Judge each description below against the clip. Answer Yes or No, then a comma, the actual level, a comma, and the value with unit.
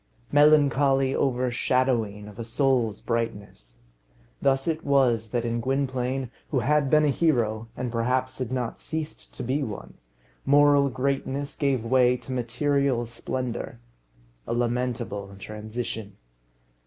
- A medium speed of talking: No, slow, 125 wpm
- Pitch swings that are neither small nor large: Yes, average, 3.0 semitones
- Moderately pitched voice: No, low, 125 Hz